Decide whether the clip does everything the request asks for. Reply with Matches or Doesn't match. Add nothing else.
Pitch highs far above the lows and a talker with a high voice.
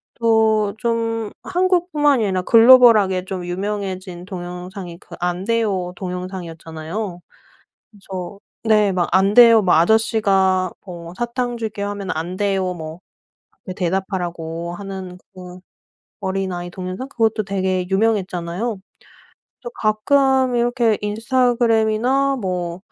Doesn't match